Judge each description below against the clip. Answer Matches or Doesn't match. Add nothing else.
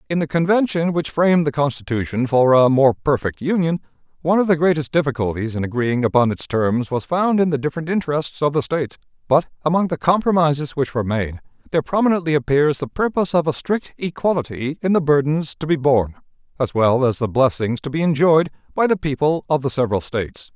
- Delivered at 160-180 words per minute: Doesn't match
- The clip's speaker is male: Matches